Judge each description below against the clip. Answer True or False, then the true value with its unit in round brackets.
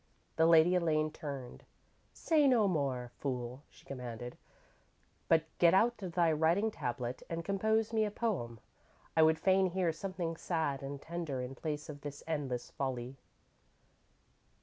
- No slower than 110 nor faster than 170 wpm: True (150 wpm)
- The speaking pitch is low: False (160 Hz)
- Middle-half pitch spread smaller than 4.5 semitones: False (5.4 semitones)